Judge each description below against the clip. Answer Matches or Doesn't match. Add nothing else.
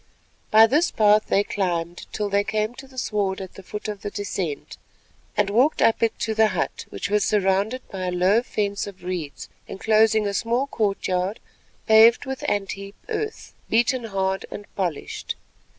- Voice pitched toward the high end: Matches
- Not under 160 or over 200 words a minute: Matches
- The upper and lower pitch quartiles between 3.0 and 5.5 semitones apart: Doesn't match